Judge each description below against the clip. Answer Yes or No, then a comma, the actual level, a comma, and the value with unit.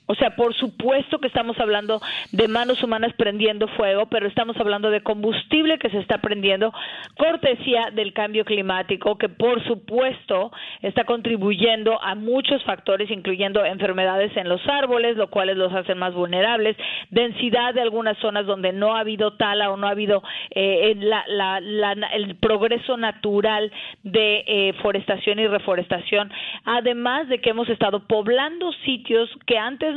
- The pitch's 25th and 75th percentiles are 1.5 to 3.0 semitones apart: Yes, narrow, 2.6 semitones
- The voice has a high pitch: Yes, high, 220 Hz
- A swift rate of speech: No, average, 160 wpm